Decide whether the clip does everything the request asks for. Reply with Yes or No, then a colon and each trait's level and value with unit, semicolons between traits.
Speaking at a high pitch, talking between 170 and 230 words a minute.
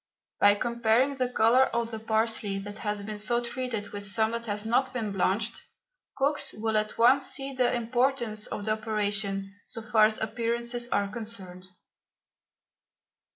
No: high, 220 Hz; average, 155 wpm